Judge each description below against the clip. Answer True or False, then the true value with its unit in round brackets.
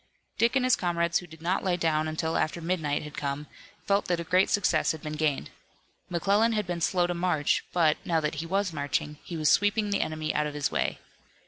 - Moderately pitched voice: True (170 Hz)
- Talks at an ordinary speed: False (225 wpm)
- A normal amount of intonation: True (3.1 semitones)